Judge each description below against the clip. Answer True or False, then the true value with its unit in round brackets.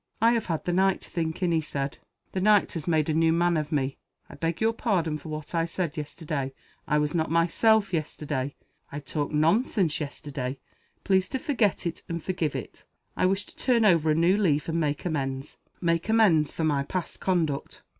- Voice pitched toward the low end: False (165 Hz)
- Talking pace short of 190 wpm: False (205 wpm)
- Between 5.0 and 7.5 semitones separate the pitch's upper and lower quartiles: False (3.7 semitones)